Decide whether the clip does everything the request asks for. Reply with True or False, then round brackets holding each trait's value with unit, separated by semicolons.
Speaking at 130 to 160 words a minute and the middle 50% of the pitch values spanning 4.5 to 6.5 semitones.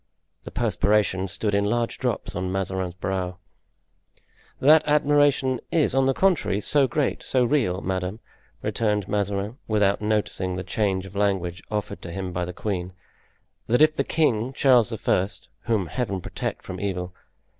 True (150 wpm; 5.0 semitones)